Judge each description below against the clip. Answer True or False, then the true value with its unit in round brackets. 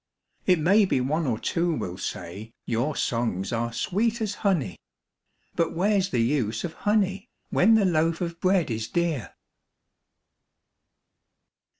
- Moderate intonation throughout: False (8.3 semitones)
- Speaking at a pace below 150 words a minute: True (135 wpm)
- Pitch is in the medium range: True (165 Hz)